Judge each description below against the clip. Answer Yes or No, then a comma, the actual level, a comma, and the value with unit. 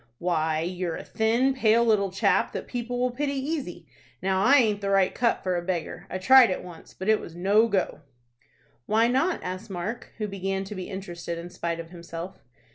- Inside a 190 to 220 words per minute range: Yes, average, 200 wpm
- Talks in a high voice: Yes, high, 195 Hz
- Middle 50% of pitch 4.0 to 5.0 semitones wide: Yes, average, 4.6 semitones